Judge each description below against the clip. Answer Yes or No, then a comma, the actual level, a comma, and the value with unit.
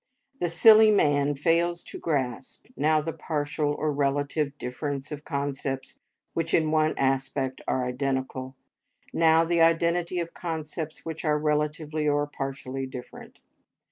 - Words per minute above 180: No, slow, 135 wpm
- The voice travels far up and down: No, average, 3.0 semitones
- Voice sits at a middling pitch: Yes, medium, 150 Hz